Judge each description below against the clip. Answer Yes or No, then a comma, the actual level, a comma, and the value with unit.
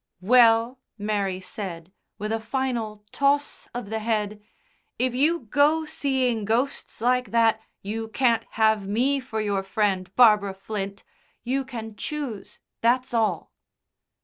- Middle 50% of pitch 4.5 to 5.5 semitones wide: No, average, 3.4 semitones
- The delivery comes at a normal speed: No, slow, 130 wpm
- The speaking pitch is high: Yes, high, 225 Hz